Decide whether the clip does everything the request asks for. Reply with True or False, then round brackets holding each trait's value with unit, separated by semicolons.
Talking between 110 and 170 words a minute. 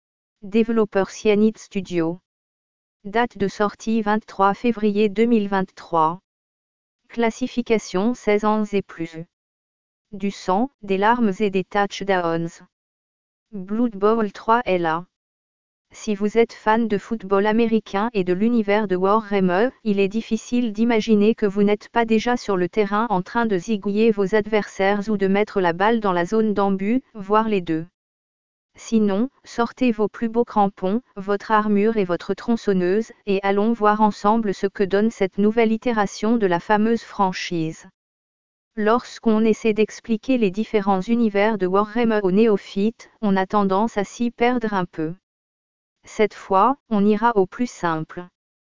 True (145 wpm)